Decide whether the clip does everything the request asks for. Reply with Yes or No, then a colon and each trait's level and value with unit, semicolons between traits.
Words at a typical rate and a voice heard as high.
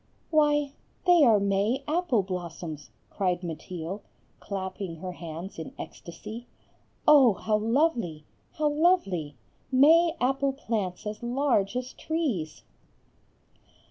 No: slow, 110 wpm; high, 215 Hz